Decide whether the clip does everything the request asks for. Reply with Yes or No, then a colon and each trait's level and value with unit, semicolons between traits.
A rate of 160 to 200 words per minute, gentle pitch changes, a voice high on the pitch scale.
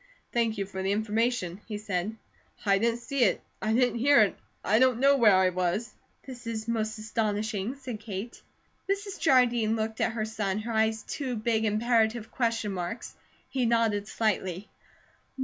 Yes: average, 165 wpm; narrow, 2.3 semitones; high, 220 Hz